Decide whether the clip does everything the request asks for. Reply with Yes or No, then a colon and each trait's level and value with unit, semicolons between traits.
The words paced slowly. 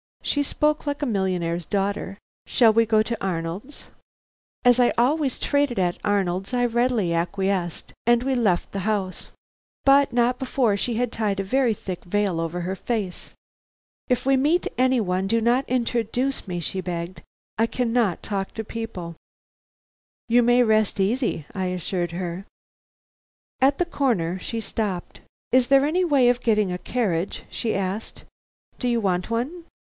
No: average, 160 wpm